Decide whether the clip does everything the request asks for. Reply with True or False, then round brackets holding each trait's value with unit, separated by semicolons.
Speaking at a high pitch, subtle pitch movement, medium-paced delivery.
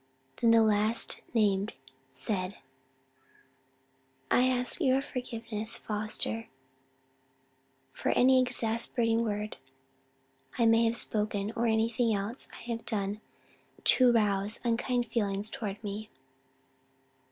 False (225 Hz; 2.1 semitones; 105 wpm)